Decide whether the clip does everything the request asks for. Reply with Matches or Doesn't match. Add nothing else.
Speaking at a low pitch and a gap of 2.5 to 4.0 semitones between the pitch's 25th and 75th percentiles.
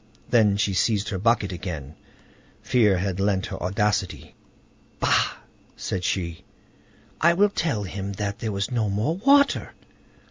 Matches